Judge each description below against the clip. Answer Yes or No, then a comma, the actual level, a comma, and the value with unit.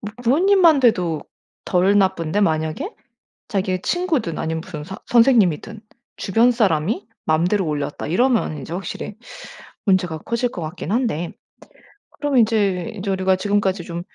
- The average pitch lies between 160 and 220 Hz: Yes, high, 190 Hz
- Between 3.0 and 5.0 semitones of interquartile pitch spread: No, wide, 5.4 semitones